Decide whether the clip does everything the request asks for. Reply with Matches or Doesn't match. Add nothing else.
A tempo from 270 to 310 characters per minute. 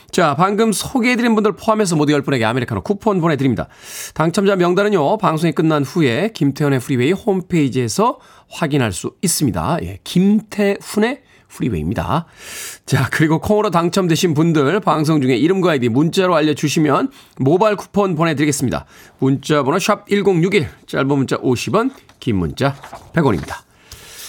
Doesn't match